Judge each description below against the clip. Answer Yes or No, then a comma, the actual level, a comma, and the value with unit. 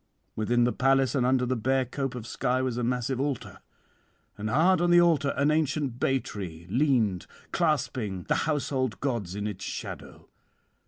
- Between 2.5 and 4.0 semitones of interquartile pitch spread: Yes, average, 3.4 semitones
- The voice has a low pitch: Yes, low, 130 Hz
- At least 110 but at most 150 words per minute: No, average, 170 wpm